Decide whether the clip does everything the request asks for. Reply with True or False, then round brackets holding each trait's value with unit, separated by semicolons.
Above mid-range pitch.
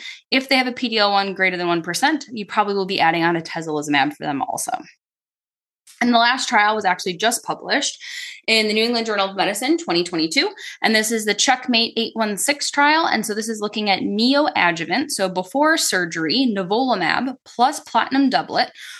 True (220 Hz)